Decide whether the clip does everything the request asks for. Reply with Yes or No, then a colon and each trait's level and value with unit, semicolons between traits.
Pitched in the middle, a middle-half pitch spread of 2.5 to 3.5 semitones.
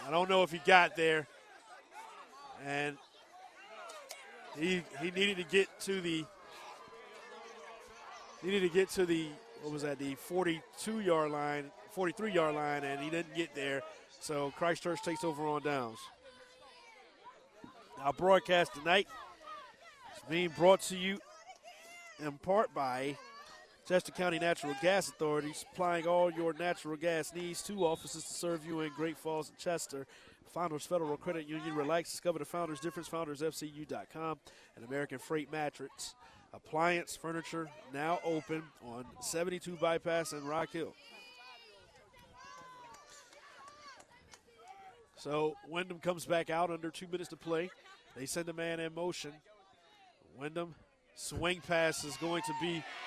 Yes: medium, 165 Hz; average, 2.9 semitones